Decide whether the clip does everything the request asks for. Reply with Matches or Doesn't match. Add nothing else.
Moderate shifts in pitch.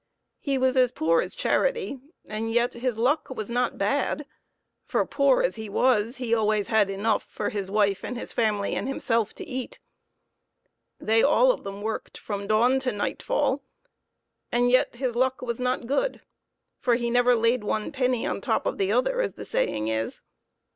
Matches